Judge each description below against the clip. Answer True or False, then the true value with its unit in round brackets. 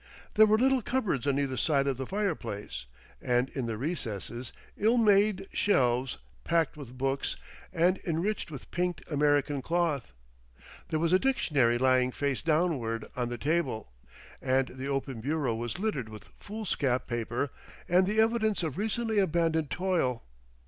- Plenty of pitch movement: True (6.5 semitones)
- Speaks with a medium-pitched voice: True (145 Hz)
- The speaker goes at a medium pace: True (150 wpm)